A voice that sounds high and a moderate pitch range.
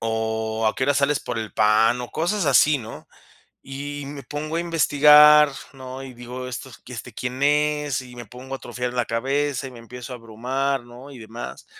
No: low, 130 Hz; average, 3.2 semitones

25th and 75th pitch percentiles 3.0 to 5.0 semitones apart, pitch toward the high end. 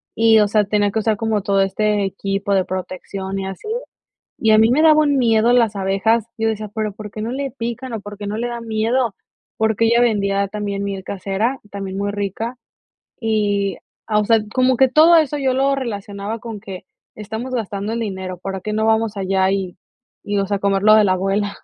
No: narrow, 2.5 semitones; high, 210 Hz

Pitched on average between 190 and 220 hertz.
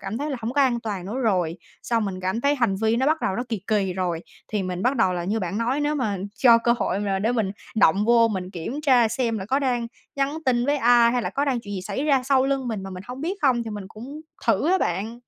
No: high, 230 Hz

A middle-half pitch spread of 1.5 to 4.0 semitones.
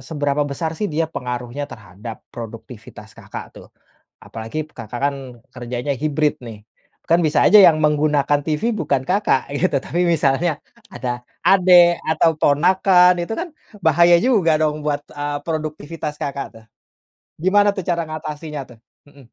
Yes: average, 3.6 semitones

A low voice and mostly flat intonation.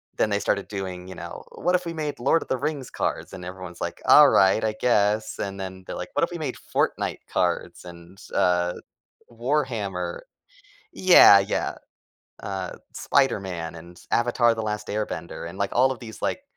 No: low, 100 Hz; average, 5.0 semitones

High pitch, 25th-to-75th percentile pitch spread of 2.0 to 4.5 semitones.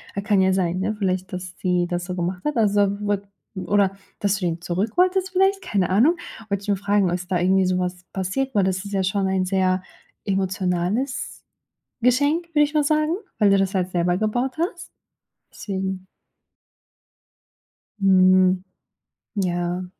Yes: high, 195 Hz; average, 2.7 semitones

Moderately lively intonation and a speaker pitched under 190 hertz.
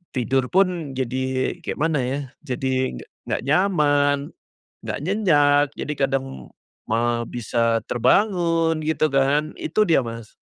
Yes: average, 3.8 semitones; medium, 140 Hz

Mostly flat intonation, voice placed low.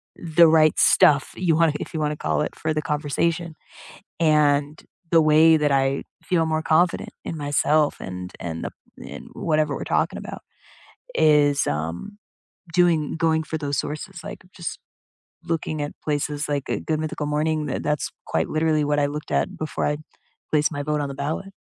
No: narrow, 1.5 semitones; medium, 150 Hz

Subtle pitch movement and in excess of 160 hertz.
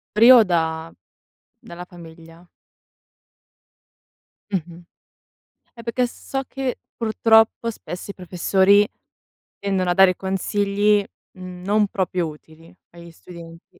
No: average, 3.6 semitones; medium, 185 Hz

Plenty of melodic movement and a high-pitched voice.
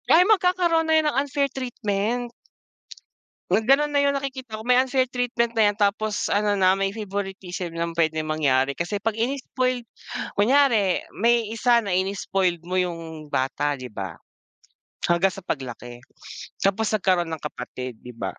Yes: wide, 6.7 semitones; high, 205 Hz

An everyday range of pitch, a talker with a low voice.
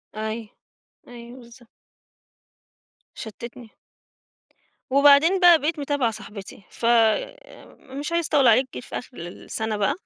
No: average, 4.6 semitones; high, 245 Hz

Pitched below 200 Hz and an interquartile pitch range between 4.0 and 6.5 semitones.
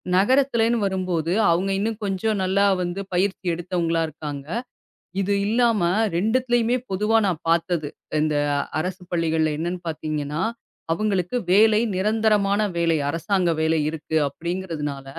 Yes: medium, 185 Hz; average, 4.3 semitones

